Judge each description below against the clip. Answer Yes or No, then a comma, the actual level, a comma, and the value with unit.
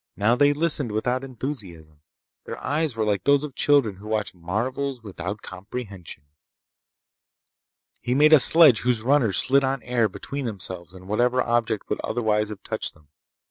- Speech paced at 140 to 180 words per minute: Yes, average, 160 wpm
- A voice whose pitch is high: No, low, 115 Hz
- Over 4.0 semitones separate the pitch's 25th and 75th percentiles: Yes, average, 5.1 semitones